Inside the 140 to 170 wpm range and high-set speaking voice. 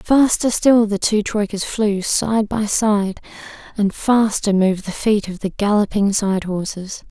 Yes: average, 160 wpm; high, 205 Hz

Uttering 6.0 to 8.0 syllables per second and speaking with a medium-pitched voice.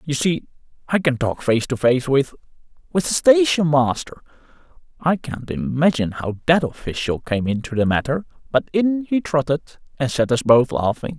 No: 4.9 syllables/s; medium, 145 Hz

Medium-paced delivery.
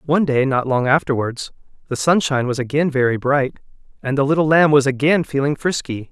Yes: average, 185 wpm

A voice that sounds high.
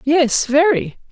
Yes: very high, 265 Hz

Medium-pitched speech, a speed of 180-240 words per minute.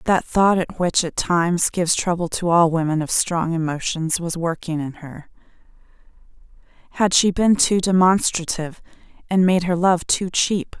No: medium, 175 Hz; average, 155 wpm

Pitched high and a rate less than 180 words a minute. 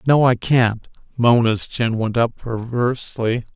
No: low, 120 Hz; slow, 135 wpm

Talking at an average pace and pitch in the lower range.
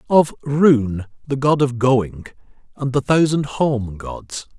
Yes: average, 145 wpm; low, 130 Hz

